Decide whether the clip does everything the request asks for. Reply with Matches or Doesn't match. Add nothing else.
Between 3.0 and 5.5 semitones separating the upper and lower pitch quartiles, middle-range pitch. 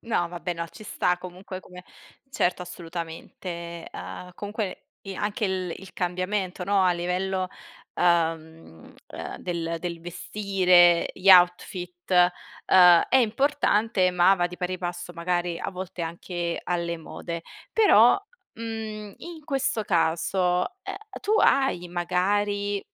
Doesn't match